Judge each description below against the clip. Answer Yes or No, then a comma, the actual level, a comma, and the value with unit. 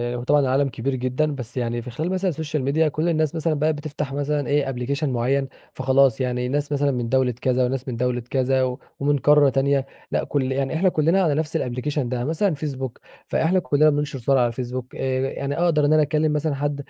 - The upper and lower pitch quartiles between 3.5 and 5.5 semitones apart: No, average, 2.8 semitones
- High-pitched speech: No, medium, 140 Hz